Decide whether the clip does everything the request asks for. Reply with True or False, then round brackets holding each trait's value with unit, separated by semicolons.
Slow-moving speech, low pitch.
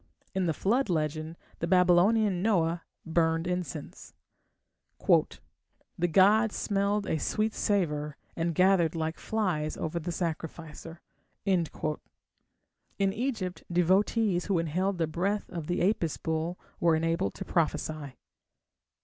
False (115 wpm; 175 Hz)